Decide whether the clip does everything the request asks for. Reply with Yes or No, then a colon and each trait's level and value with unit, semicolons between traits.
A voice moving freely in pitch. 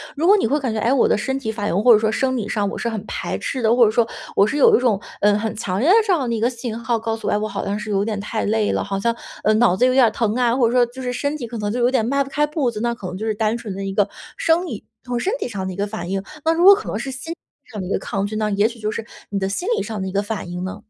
No: average, 3.6 semitones